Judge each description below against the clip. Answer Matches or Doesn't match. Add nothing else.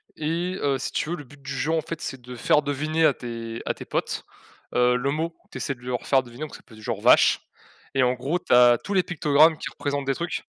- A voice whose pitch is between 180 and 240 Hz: Doesn't match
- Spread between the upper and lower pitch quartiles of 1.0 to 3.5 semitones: Doesn't match